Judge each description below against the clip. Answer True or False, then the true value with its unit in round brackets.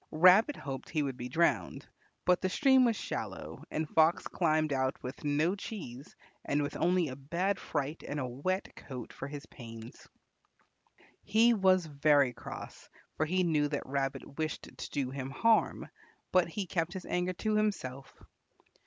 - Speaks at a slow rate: False (165 wpm)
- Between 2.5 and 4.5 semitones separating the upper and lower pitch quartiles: False (5.1 semitones)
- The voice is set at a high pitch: False (155 Hz)